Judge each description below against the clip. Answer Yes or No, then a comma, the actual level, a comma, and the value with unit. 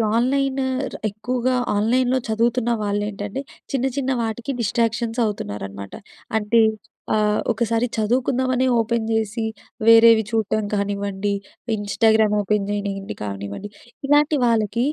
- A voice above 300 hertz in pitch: No, high, 225 Hz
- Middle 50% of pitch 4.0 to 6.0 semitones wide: No, average, 2.9 semitones